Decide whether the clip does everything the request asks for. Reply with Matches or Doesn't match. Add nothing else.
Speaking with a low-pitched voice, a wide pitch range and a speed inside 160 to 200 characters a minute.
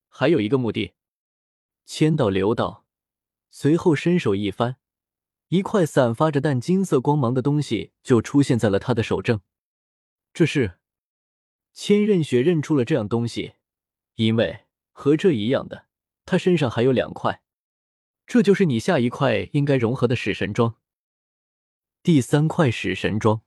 Doesn't match